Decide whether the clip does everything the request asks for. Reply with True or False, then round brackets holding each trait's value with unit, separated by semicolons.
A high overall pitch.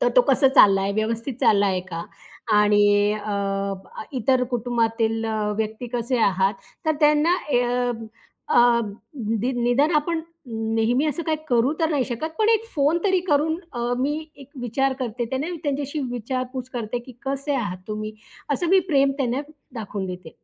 True (245 Hz)